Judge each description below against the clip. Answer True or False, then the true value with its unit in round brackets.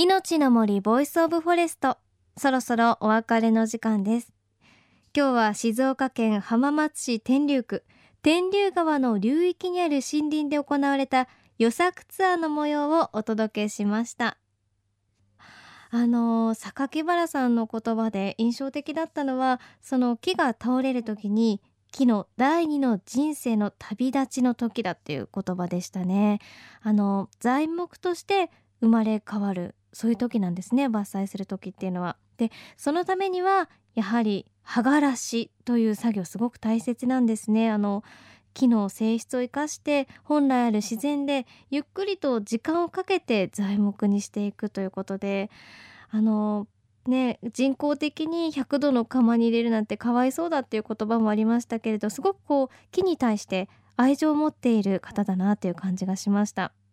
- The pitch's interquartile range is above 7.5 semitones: False (5.3 semitones)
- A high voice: True (235 Hz)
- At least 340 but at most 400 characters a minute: False (315 characters per minute)